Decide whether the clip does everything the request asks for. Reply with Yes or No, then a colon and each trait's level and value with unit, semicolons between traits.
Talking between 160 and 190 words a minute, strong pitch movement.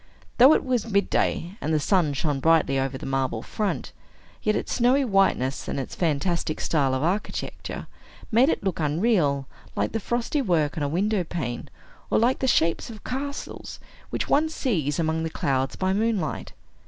Yes: average, 175 wpm; wide, 7.5 semitones